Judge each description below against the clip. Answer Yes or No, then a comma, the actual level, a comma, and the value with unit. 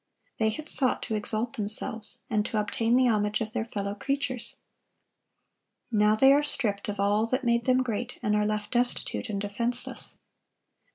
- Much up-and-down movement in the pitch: No, average, 2.9 semitones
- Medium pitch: No, high, 220 Hz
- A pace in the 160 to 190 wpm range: Yes, average, 170 wpm